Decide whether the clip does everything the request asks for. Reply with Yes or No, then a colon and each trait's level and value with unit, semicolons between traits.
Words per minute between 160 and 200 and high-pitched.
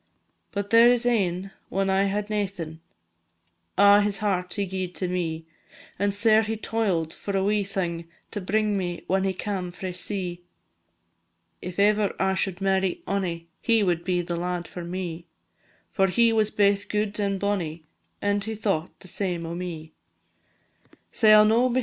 Yes: average, 175 wpm; high, 195 Hz